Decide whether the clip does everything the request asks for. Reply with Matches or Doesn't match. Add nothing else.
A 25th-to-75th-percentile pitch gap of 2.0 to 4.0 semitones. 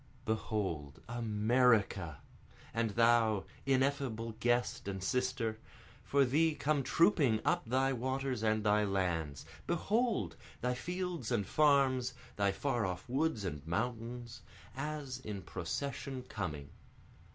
Doesn't match